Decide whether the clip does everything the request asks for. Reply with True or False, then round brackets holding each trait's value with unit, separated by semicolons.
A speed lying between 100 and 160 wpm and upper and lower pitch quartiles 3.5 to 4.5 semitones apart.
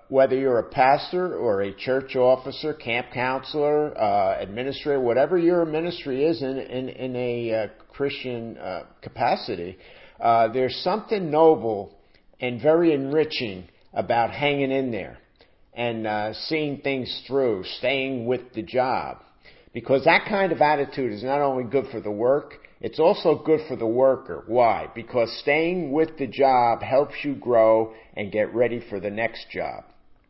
True (155 wpm; 4.1 semitones)